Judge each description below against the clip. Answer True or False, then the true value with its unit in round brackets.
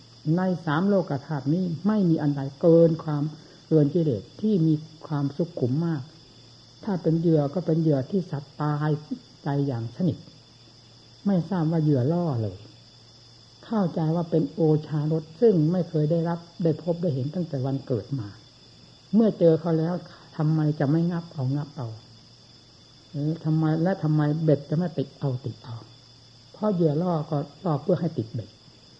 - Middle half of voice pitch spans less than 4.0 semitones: False (4.3 semitones)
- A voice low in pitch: False (155 Hz)